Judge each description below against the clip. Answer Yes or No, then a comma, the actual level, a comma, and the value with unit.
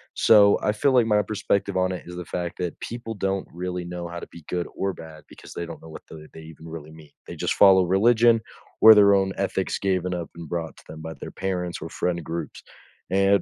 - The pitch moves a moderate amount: Yes, average, 3.0 semitones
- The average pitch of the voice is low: Yes, very low, 90 Hz